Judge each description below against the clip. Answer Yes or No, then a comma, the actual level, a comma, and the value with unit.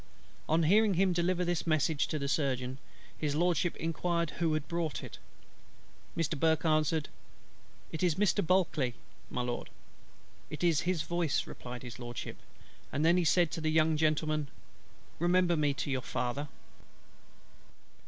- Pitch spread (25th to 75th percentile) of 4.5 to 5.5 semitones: No, average, 3.0 semitones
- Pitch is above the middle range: No, medium, 160 Hz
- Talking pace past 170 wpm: No, average, 145 wpm